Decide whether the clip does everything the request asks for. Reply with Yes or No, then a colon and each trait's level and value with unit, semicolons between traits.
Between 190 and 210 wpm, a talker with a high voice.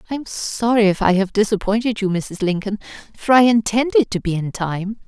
Yes: average, 200 wpm; high, 210 Hz